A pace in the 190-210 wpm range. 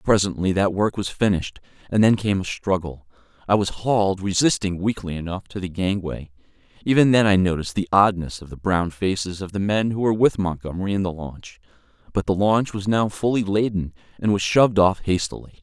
Yes: average, 195 wpm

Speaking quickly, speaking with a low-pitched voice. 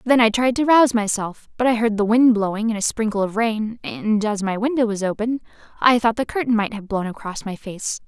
No: fast, 245 wpm; high, 220 Hz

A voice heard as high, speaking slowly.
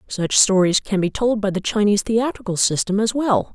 No: high, 205 Hz; fast, 205 wpm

